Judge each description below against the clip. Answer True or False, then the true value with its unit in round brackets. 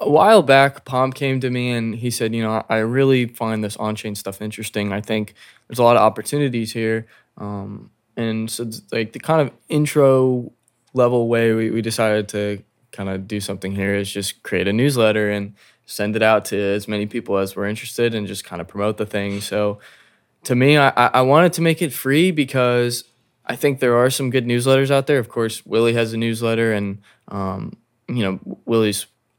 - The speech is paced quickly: True (210 wpm)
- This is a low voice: True (115 Hz)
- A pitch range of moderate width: True (3.4 semitones)